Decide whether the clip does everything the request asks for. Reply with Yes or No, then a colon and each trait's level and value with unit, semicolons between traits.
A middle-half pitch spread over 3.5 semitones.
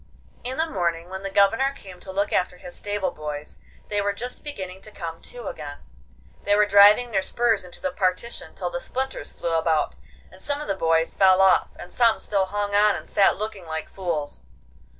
No: average, 3.2 semitones